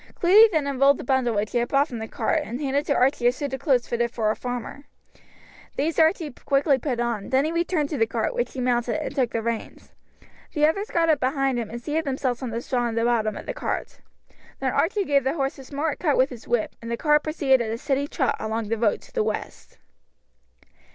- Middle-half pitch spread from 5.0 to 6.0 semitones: No, average, 3.8 semitones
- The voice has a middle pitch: No, very high, 265 Hz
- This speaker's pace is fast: Yes, fast, 245 wpm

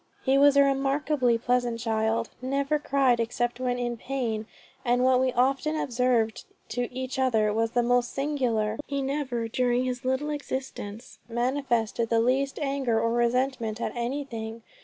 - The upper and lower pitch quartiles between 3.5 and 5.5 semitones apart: No, average, 2.8 semitones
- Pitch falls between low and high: No, very high, 250 Hz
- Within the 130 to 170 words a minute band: Yes, average, 155 wpm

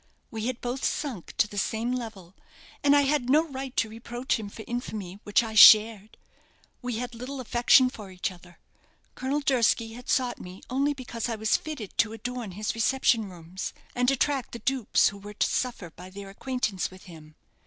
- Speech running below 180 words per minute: No, average, 190 wpm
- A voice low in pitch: No, high, 230 Hz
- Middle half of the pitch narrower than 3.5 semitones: No, average, 4.0 semitones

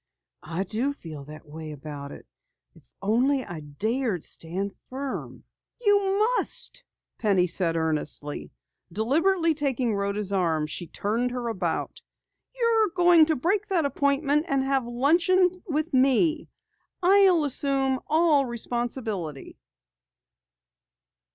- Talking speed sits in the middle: No, slow, 120 wpm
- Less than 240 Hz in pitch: No, very high, 255 Hz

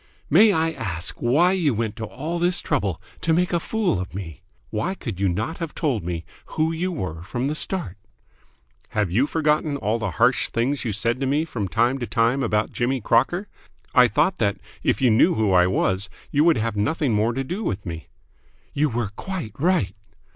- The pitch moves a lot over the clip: Yes, wide, 7.5 semitones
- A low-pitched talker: Yes, low, 120 Hz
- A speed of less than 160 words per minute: No, fast, 205 wpm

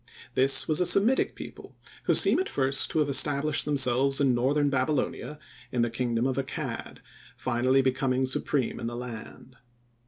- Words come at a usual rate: Yes, average, 160 wpm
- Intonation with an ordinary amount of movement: No, narrow, 2.3 semitones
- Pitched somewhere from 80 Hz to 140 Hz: Yes, low, 135 Hz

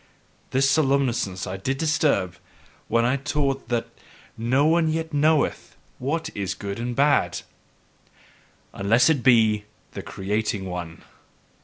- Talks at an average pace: No, slow, 125 wpm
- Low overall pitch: Yes, low, 125 Hz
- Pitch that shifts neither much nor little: No, wide, 5.7 semitones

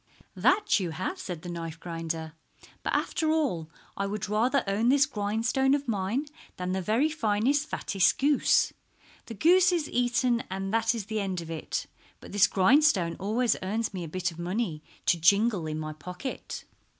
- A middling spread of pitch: No, wide, 6.0 semitones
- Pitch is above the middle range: Yes, high, 205 Hz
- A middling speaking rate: Yes, average, 175 wpm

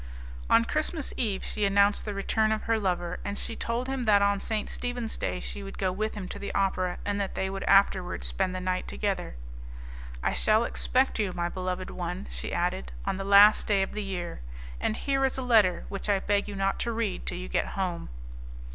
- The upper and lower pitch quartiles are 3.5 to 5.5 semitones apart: No, average, 2.7 semitones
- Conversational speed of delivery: No, fast, 220 wpm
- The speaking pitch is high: Yes, high, 200 Hz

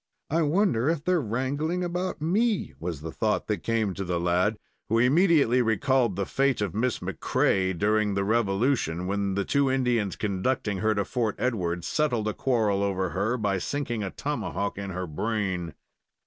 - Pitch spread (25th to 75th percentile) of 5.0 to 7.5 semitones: Yes, wide, 5.4 semitones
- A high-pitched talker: No, low, 110 Hz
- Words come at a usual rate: Yes, average, 175 wpm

